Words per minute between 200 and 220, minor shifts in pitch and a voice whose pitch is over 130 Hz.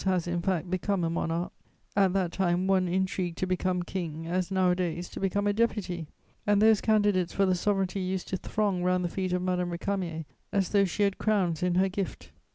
Yes: fast, 205 wpm; narrow, 1.9 semitones; medium, 185 Hz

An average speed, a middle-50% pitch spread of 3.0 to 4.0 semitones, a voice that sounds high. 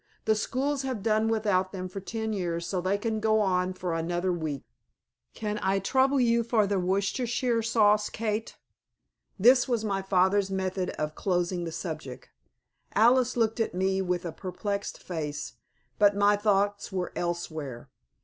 Yes: average, 155 wpm; average, 3.4 semitones; high, 200 Hz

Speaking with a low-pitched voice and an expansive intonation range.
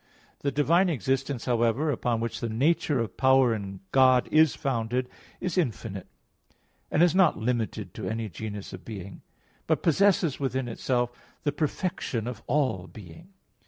No: low, 125 Hz; average, 4.8 semitones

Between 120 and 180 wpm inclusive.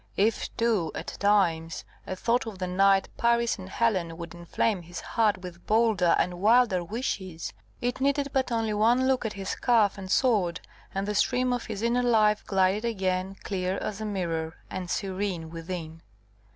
Yes: average, 170 wpm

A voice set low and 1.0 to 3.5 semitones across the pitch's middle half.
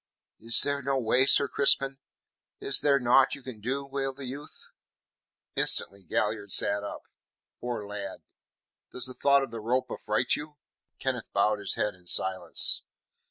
No: low, 125 Hz; average, 4.6 semitones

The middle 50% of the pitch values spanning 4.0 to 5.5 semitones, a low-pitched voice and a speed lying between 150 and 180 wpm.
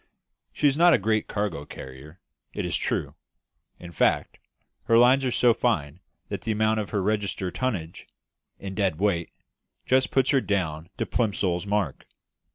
Yes: average, 5.1 semitones; low, 100 Hz; average, 165 wpm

